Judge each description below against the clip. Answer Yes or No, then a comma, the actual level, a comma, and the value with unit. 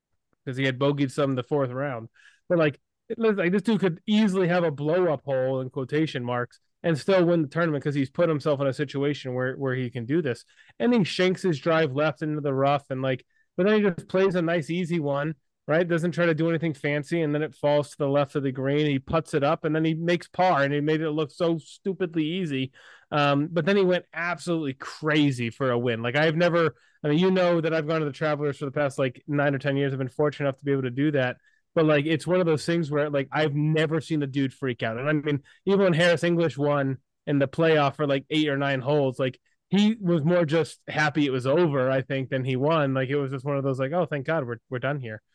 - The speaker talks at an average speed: No, fast, 265 wpm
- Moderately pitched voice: Yes, medium, 150 Hz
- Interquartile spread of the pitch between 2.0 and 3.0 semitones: No, average, 3.6 semitones